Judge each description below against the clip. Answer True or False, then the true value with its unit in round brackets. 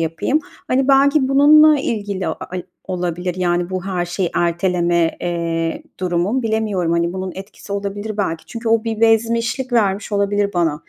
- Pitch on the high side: True (195 Hz)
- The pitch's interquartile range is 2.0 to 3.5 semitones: False (4.5 semitones)